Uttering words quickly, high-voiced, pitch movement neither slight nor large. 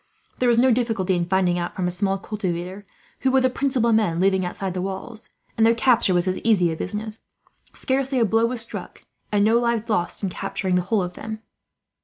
Yes: fast, 215 wpm; high, 210 Hz; average, 4.0 semitones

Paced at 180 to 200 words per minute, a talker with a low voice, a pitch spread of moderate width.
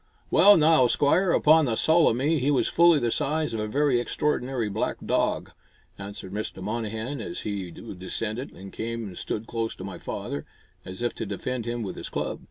No: average, 195 wpm; low, 115 Hz; wide, 5.7 semitones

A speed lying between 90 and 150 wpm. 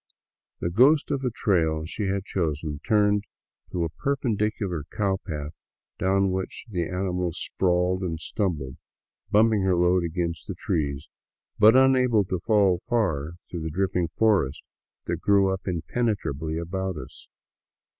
Yes: slow, 135 wpm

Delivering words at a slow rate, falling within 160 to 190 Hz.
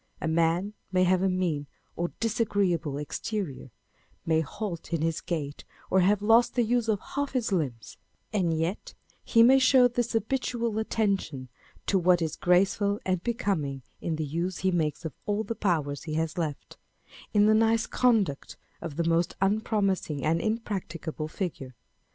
No: average, 170 wpm; medium, 185 Hz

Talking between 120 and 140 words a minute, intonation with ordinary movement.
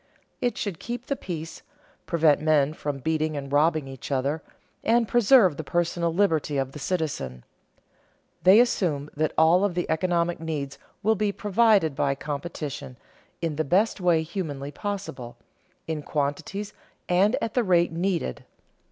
No: average, 150 wpm; average, 4.8 semitones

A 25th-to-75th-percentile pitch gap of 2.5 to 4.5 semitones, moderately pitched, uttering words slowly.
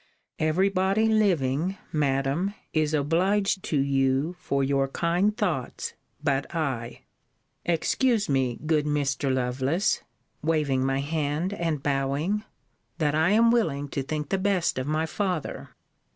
No: average, 5.3 semitones; medium, 155 Hz; slow, 130 wpm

